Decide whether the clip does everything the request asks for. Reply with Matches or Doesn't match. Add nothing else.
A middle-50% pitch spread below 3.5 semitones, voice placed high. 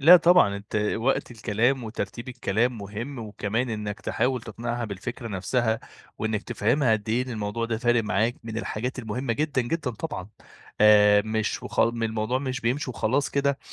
Doesn't match